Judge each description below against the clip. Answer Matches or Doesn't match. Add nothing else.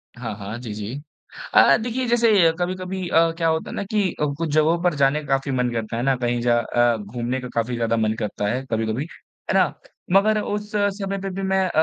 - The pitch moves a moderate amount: Doesn't match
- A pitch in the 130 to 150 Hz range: Matches